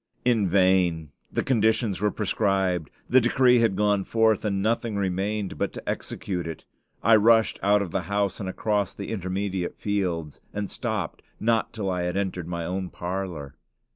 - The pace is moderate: Yes, average, 165 wpm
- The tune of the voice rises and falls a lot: No, average, 2.9 semitones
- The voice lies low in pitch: Yes, low, 100 Hz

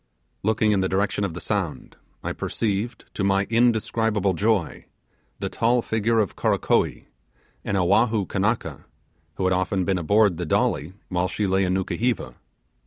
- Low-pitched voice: Yes, low, 100 Hz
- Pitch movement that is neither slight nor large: Yes, average, 3.1 semitones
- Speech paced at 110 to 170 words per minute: Yes, average, 155 wpm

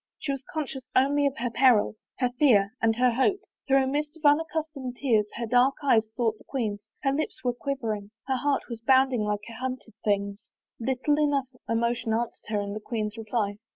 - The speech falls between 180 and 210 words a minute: Yes, average, 195 wpm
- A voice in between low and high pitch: No, very high, 250 Hz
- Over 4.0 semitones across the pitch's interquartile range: No, average, 3.7 semitones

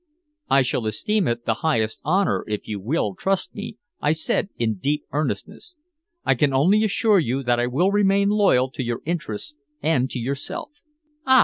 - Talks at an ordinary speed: Yes, average, 180 wpm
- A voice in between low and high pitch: Yes, medium, 145 Hz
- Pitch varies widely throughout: Yes, wide, 8.3 semitones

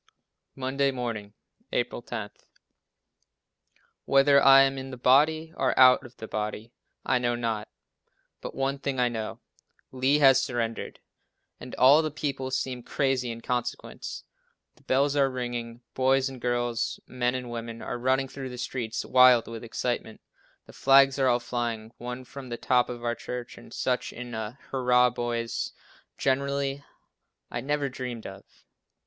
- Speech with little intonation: Yes, narrow, 2.1 semitones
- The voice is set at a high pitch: No, low, 125 Hz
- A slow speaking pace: No, average, 155 wpm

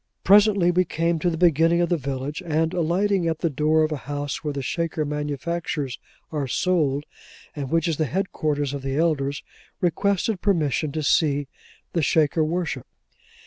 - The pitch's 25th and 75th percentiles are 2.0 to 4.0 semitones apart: Yes, average, 3.1 semitones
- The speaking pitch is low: No, medium, 160 Hz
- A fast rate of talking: No, average, 170 wpm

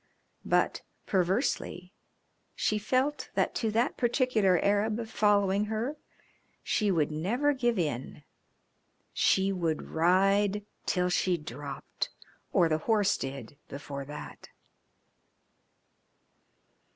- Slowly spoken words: Yes, slow, 100 wpm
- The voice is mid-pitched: No, high, 195 Hz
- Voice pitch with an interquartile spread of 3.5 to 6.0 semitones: Yes, average, 5.2 semitones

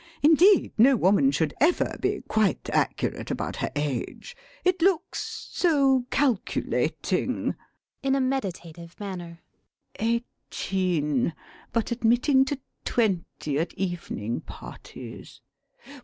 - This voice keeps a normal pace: No, slow, 100 wpm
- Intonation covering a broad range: Yes, wide, 7.9 semitones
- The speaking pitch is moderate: No, high, 225 Hz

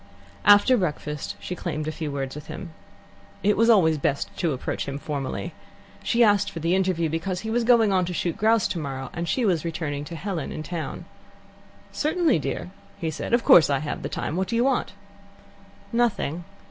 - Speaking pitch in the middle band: Yes, medium, 175 Hz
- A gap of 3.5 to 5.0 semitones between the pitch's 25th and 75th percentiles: No, wide, 5.4 semitones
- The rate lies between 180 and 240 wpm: Yes, average, 195 wpm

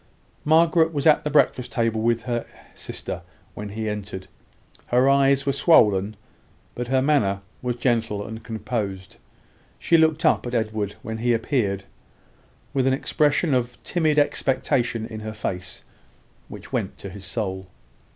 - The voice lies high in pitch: No, low, 120 Hz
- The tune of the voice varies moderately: Yes, average, 4.6 semitones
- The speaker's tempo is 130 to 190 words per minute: Yes, average, 150 wpm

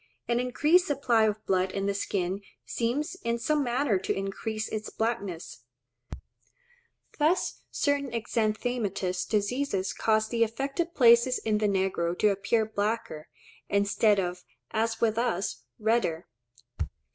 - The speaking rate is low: Yes, slow, 125 wpm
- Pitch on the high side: Yes, high, 220 Hz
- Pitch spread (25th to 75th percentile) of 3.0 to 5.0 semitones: Yes, average, 3.4 semitones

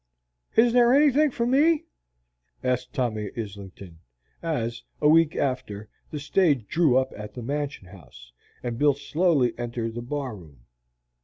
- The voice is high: No, low, 130 Hz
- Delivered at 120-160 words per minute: Yes, average, 145 wpm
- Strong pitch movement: Yes, wide, 6.9 semitones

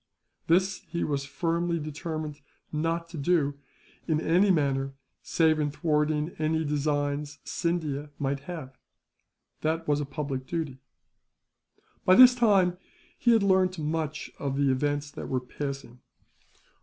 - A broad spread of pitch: No, average, 2.9 semitones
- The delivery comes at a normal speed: No, slow, 130 wpm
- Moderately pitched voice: Yes, medium, 155 Hz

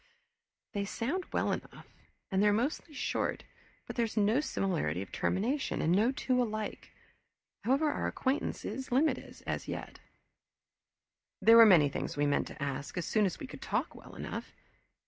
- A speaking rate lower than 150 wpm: No, average, 165 wpm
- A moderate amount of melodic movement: No, wide, 6.2 semitones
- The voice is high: Yes, high, 215 Hz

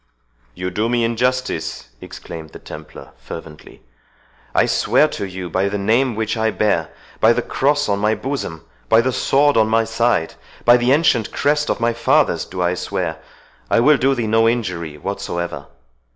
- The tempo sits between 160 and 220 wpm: Yes, average, 165 wpm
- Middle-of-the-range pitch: No, low, 110 Hz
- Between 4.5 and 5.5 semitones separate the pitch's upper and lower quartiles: Yes, average, 5.1 semitones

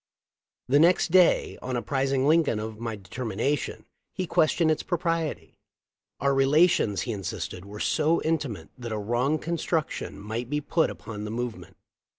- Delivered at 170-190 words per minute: No, average, 150 wpm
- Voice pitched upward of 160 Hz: No, low, 135 Hz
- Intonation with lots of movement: Yes, wide, 6.1 semitones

